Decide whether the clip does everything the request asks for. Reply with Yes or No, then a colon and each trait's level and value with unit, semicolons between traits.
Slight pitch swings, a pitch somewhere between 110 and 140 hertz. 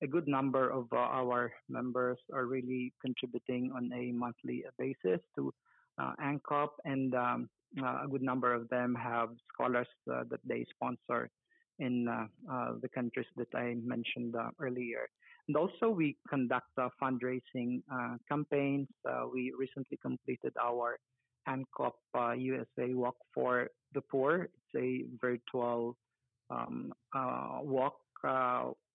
Yes: narrow, 1.5 semitones; low, 125 Hz